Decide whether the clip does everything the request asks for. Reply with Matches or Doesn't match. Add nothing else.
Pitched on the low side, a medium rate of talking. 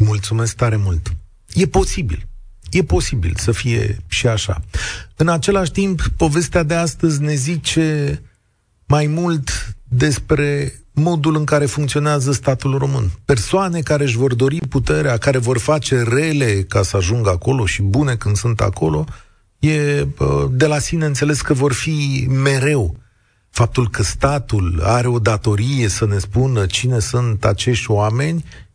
Matches